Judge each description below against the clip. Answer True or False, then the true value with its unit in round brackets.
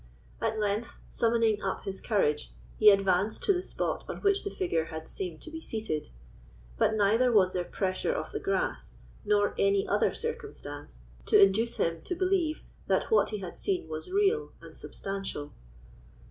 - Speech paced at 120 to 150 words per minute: False (170 wpm)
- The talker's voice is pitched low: False (210 Hz)